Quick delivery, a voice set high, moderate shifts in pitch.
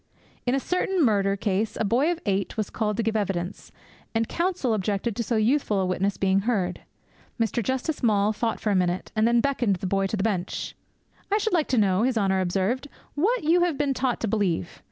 Yes: fast, 215 wpm; high, 220 Hz; average, 5.0 semitones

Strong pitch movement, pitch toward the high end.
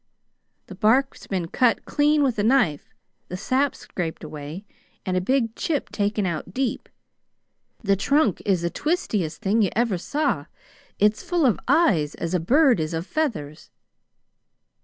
Yes: wide, 7.6 semitones; high, 210 Hz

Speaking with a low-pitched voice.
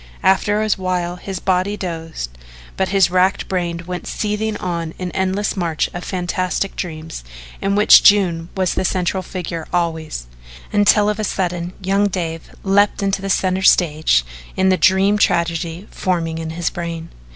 No: medium, 185 Hz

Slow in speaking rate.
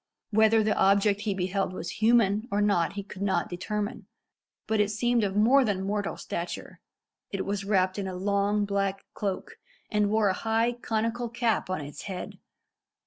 No: average, 175 wpm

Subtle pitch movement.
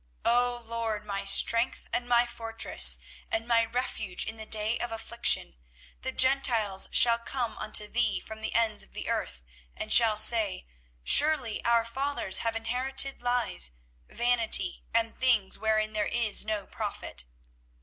Yes: narrow, 2.0 semitones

